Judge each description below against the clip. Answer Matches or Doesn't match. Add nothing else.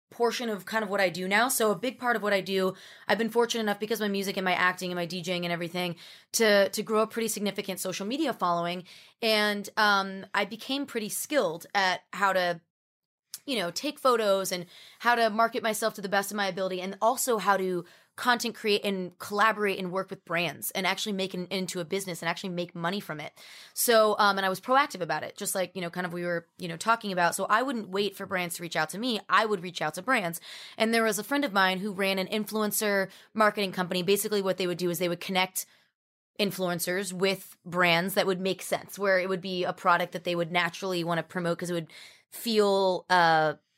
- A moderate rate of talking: Doesn't match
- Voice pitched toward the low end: Doesn't match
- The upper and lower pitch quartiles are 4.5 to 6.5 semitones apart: Doesn't match